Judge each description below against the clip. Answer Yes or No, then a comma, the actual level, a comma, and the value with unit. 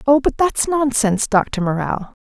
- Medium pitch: No, high, 245 Hz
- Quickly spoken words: No, average, 160 wpm